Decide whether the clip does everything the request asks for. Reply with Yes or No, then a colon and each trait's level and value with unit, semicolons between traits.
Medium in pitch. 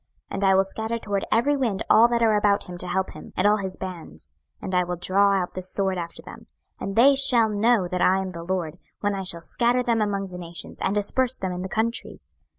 No: high, 195 Hz